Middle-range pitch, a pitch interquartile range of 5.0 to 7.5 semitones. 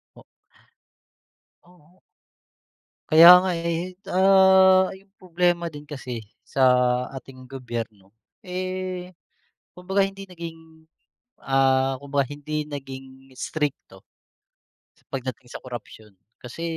Yes: medium, 155 Hz; wide, 5.4 semitones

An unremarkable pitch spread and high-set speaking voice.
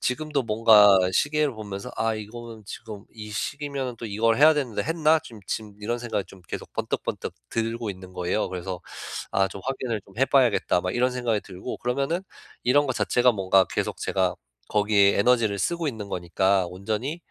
No: average, 4.4 semitones; low, 115 Hz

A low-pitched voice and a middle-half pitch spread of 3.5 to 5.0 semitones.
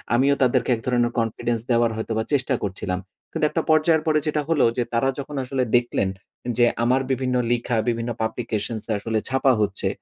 No: low, 120 Hz; average, 2.8 semitones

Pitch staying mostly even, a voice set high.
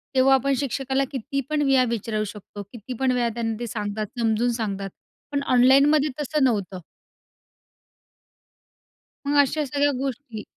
No: average, 4.1 semitones; very high, 255 Hz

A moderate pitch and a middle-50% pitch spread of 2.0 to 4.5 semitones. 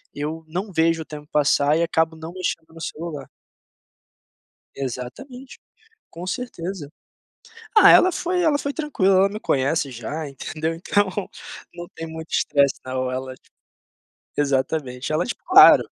No: medium, 160 Hz; average, 5.0 semitones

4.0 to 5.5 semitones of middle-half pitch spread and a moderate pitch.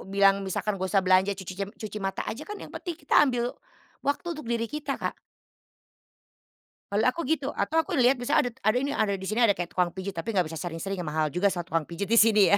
No: average, 4.7 semitones; high, 200 Hz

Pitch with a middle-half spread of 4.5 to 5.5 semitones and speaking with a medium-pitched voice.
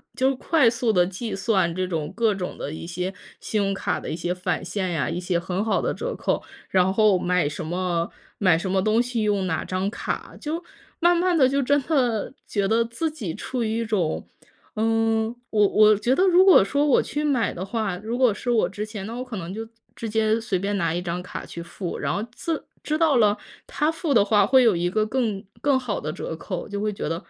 No: average, 4.9 semitones; high, 215 Hz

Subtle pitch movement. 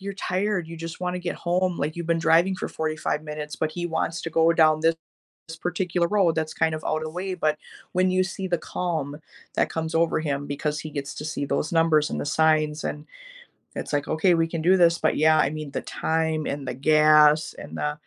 Yes: narrow, 2.1 semitones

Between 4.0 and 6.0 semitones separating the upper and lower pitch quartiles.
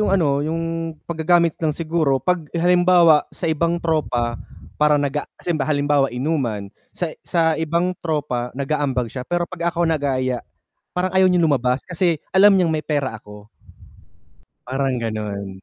Yes: average, 4.5 semitones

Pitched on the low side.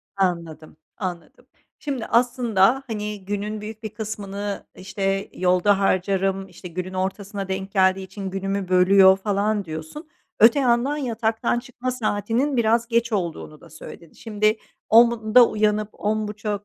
No: high, 205 Hz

